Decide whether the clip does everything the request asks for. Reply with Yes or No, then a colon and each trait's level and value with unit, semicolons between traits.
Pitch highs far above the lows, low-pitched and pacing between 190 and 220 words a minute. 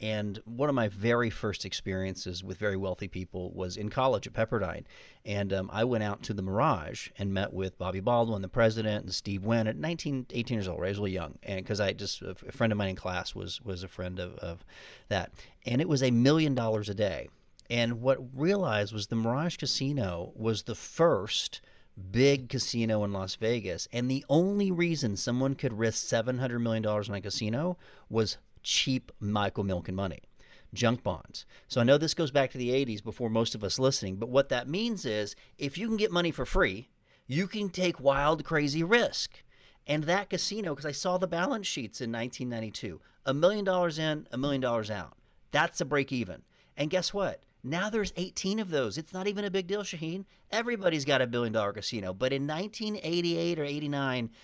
Yes: wide, 6.7 semitones; low, 120 Hz; fast, 205 wpm